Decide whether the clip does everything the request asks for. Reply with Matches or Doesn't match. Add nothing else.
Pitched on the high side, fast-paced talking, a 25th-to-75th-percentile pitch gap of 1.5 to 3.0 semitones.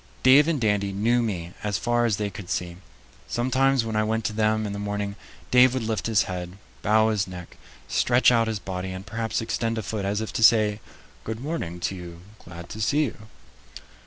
Doesn't match